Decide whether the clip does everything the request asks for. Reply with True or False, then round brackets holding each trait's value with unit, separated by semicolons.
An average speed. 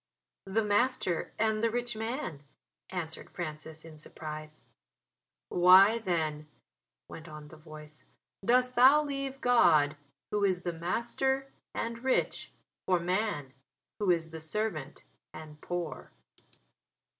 False (120 wpm)